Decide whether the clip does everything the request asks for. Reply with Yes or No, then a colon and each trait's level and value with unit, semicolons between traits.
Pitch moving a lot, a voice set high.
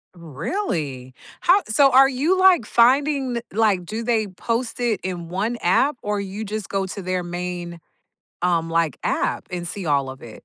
Yes: wide, 5.8 semitones; high, 200 Hz